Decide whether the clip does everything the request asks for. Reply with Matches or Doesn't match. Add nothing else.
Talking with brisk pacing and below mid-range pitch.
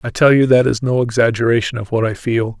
Matches